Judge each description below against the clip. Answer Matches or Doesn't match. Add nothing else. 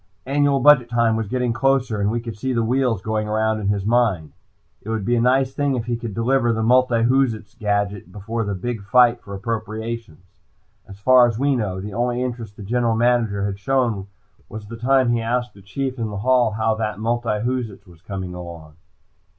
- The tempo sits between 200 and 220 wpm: Matches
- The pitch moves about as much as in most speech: Matches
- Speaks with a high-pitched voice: Doesn't match